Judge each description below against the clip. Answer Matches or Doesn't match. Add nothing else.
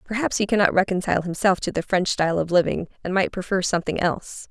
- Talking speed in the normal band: Doesn't match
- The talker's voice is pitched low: Doesn't match